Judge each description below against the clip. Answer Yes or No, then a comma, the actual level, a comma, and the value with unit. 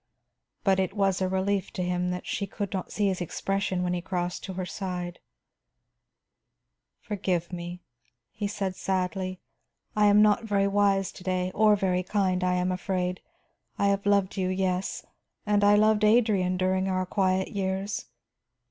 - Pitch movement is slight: Yes, narrow, 1.7 semitones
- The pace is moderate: Yes, average, 165 wpm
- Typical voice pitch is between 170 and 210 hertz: Yes, high, 190 Hz